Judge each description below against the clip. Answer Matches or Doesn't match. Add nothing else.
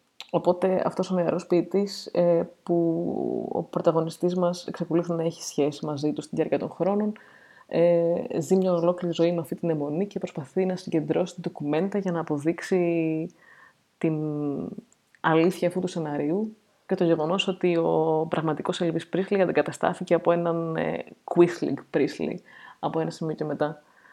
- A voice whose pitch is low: Doesn't match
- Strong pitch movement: Doesn't match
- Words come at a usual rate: Matches